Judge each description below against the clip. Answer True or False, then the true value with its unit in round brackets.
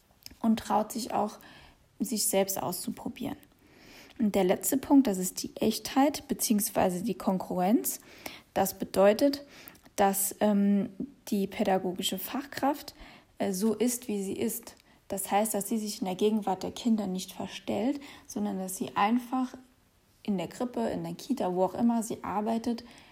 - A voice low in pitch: False (215 Hz)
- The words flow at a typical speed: True (150 wpm)